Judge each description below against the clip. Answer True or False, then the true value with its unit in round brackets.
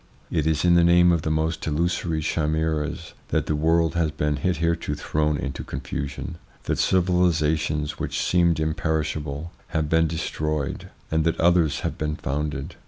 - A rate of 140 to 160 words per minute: True (155 wpm)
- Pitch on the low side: True (80 Hz)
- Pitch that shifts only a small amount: True (1.8 semitones)